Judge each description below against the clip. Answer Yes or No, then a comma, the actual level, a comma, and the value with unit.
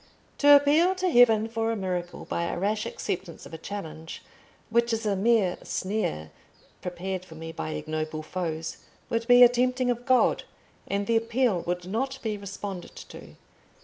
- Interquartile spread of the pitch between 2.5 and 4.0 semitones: No, average, 5.3 semitones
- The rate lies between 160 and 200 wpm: Yes, average, 170 wpm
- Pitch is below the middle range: No, high, 205 Hz